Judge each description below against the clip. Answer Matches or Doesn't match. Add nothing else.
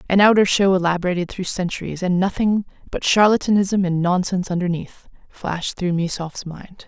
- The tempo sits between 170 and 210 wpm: Doesn't match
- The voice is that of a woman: Matches